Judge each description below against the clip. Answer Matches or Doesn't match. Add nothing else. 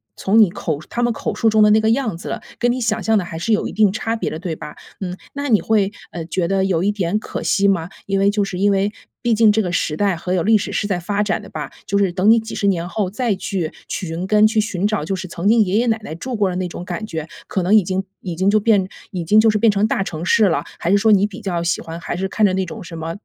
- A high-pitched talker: Matches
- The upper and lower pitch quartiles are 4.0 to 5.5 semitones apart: Doesn't match